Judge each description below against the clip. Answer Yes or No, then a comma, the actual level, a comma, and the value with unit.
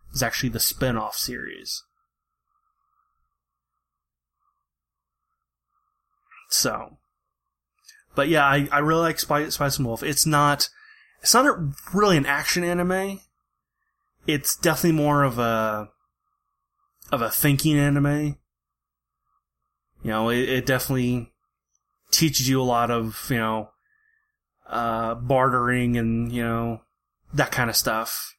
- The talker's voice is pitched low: No, medium, 150 Hz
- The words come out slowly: Yes, slow, 115 wpm